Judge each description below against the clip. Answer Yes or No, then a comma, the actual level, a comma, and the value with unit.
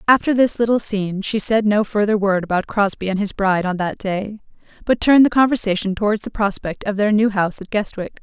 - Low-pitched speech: No, high, 205 Hz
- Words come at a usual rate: No, fast, 220 wpm